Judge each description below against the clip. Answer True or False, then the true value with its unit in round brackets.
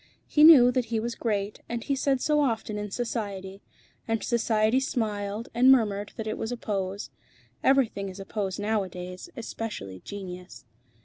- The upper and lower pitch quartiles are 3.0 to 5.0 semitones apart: True (3.3 semitones)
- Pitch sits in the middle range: False (220 Hz)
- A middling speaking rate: True (165 wpm)